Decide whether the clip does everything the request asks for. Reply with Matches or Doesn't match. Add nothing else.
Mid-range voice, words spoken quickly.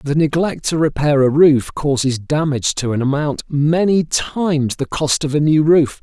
Doesn't match